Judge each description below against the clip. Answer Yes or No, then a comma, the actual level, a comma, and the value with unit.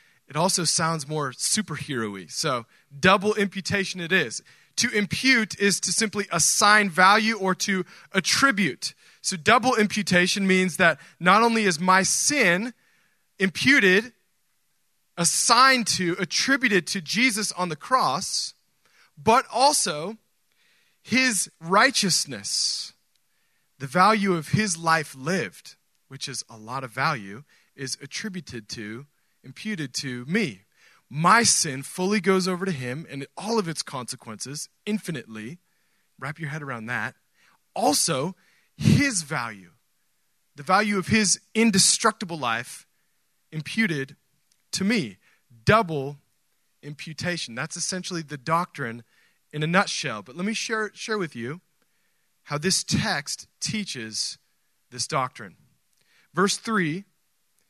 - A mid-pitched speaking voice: Yes, medium, 180 Hz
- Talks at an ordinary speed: No, slow, 120 wpm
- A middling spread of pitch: No, wide, 6.0 semitones